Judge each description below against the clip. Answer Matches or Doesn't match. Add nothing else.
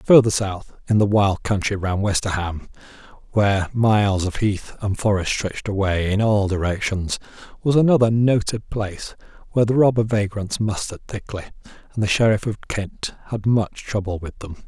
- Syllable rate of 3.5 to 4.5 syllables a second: Doesn't match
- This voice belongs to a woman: Doesn't match